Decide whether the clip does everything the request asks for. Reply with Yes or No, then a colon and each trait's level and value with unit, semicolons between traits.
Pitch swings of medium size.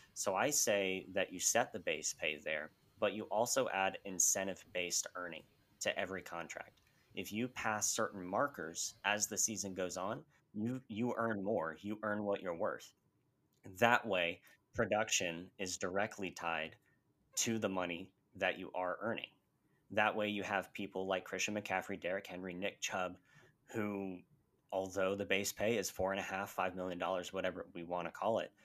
No: narrow, 2.2 semitones